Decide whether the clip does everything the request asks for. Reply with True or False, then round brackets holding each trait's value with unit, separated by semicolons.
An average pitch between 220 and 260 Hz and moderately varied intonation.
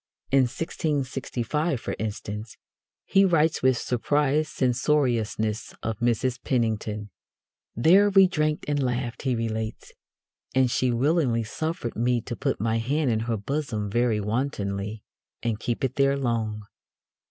False (120 Hz; 4.3 semitones)